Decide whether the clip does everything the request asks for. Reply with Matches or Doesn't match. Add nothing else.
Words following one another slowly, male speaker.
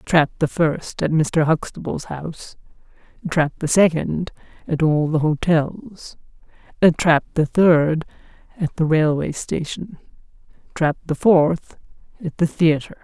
Doesn't match